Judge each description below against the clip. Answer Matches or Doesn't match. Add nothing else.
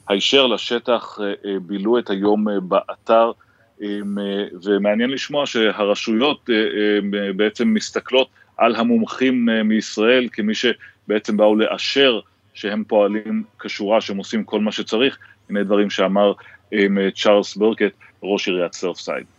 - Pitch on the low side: Matches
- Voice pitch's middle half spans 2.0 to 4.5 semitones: Matches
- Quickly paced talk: Doesn't match